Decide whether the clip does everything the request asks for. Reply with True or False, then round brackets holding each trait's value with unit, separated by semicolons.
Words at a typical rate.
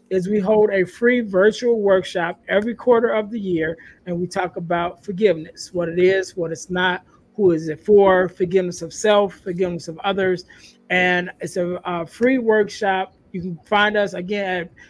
True (180 wpm)